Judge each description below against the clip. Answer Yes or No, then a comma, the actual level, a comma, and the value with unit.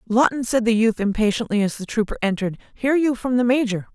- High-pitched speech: Yes, high, 230 Hz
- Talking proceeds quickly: Yes, fast, 215 wpm